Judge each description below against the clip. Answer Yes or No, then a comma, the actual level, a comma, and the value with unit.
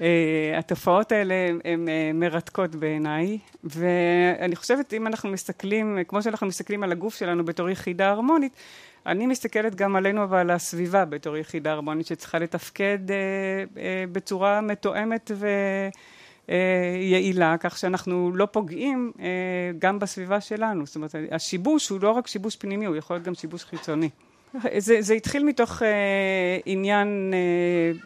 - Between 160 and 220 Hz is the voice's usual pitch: Yes, high, 190 Hz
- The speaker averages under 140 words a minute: No, average, 145 wpm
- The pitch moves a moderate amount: Yes, average, 3.0 semitones